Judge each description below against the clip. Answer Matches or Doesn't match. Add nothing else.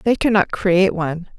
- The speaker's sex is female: Matches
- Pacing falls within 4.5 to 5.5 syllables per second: Doesn't match